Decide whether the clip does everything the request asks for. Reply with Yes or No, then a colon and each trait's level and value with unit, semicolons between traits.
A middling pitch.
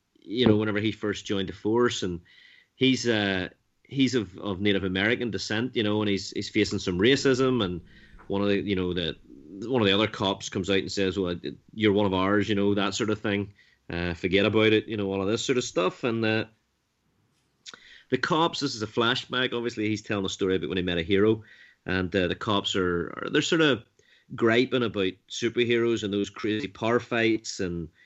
No: low, 105 Hz